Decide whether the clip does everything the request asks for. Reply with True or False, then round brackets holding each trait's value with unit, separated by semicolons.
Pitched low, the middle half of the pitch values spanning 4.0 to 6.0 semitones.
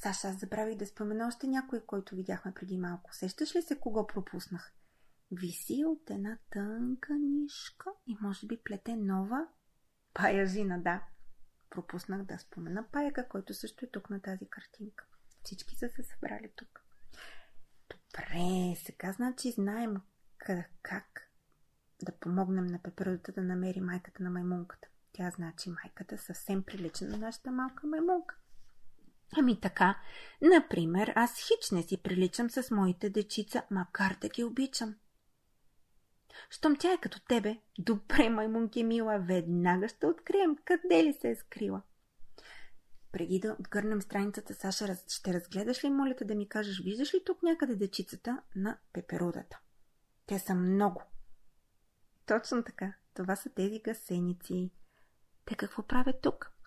False (205 Hz; 4.7 semitones)